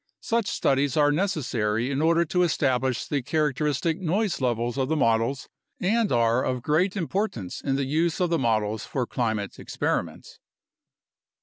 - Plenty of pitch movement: Yes, wide, 5.7 semitones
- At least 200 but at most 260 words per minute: No, average, 165 wpm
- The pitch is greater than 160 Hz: No, medium, 140 Hz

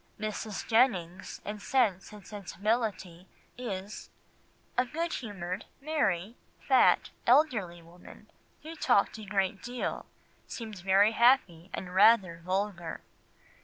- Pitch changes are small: No, average, 4.2 semitones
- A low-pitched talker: No, high, 205 Hz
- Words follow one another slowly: Yes, slow, 110 wpm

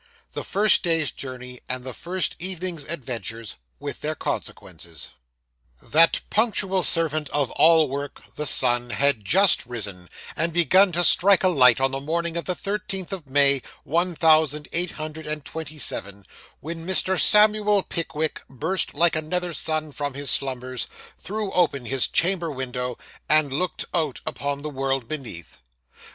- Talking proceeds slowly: No, average, 155 wpm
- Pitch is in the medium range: Yes, medium, 155 Hz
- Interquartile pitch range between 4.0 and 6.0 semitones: Yes, average, 4.7 semitones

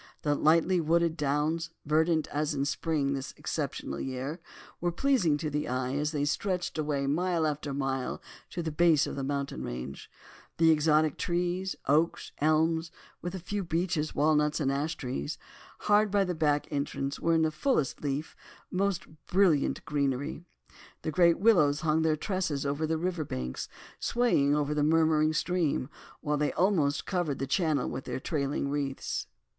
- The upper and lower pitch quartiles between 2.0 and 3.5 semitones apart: Yes, average, 3.0 semitones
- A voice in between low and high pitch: Yes, medium, 155 Hz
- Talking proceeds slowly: No, average, 170 wpm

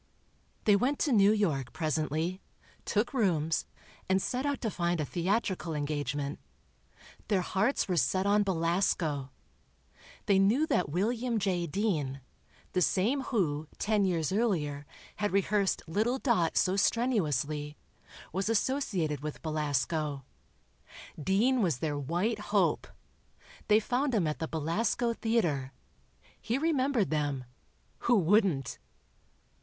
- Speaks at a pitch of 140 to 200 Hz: Yes, medium, 185 Hz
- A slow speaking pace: Yes, slow, 120 wpm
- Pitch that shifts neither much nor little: No, wide, 6.2 semitones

